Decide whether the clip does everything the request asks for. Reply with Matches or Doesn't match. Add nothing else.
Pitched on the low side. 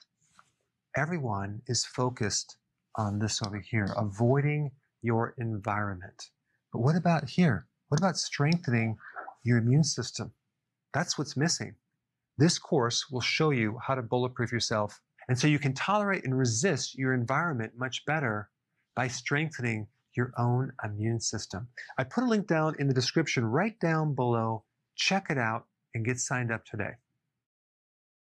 Matches